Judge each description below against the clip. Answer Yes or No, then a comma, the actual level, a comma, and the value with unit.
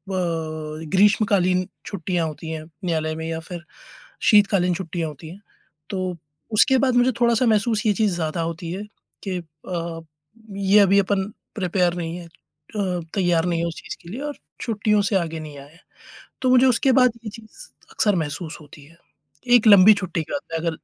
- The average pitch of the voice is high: No, medium, 180 Hz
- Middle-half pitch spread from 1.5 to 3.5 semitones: No, average, 4.1 semitones